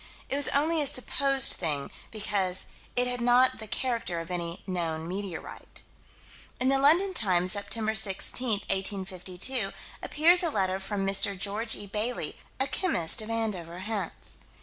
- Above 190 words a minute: No, average, 150 wpm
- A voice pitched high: Yes, high, 210 Hz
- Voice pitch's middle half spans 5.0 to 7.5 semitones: Yes, wide, 5.4 semitones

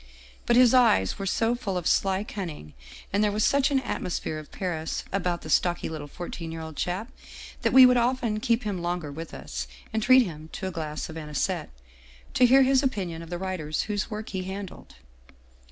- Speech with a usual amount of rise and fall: No, wide, 5.9 semitones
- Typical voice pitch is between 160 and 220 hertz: Yes, high, 190 Hz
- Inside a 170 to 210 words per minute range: Yes, fast, 205 wpm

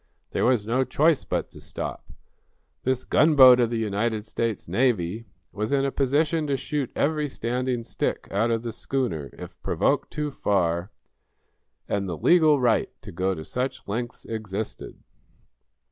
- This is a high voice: No, low, 120 Hz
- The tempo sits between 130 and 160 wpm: Yes, average, 155 wpm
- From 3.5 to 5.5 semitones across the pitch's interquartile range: Yes, average, 4.6 semitones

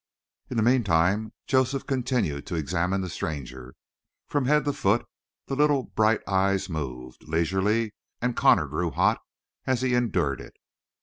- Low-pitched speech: Yes, low, 100 Hz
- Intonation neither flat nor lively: No, wide, 7.5 semitones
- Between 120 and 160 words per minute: Yes, average, 145 wpm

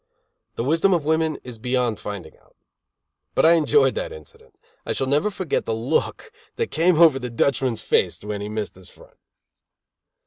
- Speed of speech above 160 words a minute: Yes, average, 175 wpm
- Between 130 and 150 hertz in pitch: Yes, medium, 140 Hz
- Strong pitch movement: Yes, wide, 6.9 semitones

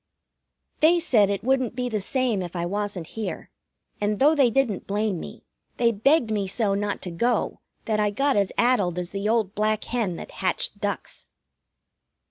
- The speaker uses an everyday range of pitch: Yes, average, 3.7 semitones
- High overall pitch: Yes, high, 215 Hz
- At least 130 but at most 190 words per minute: Yes, average, 180 wpm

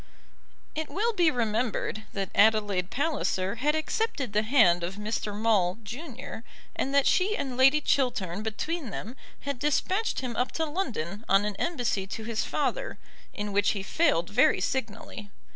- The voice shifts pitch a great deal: Yes, wide, 6.2 semitones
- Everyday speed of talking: Yes, average, 160 wpm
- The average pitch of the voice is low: No, high, 230 Hz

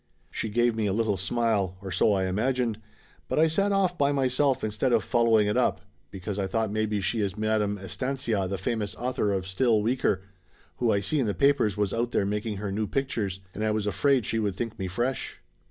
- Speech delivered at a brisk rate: Yes, fast, 235 wpm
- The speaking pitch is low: Yes, low, 110 Hz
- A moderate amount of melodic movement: Yes, average, 3.3 semitones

